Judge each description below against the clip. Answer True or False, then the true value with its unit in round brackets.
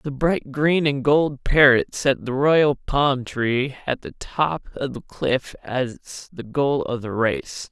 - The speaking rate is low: False (180 wpm)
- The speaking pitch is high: False (135 Hz)